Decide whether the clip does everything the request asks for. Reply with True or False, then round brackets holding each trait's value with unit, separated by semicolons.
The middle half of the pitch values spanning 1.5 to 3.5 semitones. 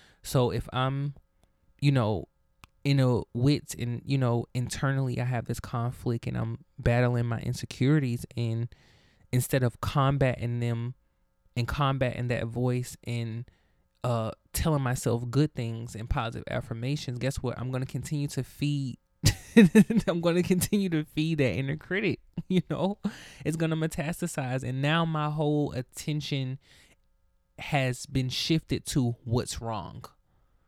False (3.9 semitones)